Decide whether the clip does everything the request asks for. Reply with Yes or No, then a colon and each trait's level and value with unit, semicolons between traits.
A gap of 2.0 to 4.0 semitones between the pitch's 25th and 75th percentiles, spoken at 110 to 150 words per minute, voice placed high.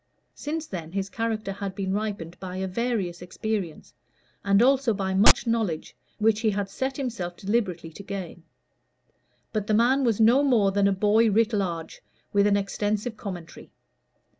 No: average, 3.1 semitones; average, 165 wpm; high, 205 Hz